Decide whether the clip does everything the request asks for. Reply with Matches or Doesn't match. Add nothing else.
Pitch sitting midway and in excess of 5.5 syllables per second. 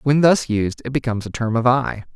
Doesn't match